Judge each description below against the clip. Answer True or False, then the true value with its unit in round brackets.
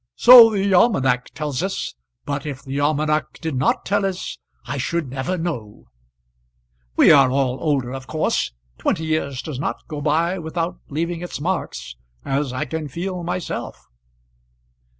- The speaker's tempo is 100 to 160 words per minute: True (150 wpm)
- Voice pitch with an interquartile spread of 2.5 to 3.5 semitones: False (4.4 semitones)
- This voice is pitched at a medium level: True (155 Hz)